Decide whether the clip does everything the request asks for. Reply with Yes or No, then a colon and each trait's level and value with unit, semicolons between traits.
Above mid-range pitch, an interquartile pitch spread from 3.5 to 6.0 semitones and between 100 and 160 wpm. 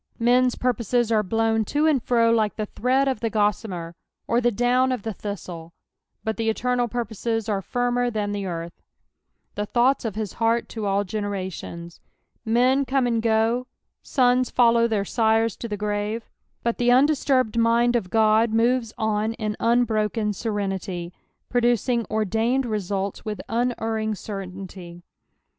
No: high, 225 Hz; narrow, 2.6 semitones; average, 155 wpm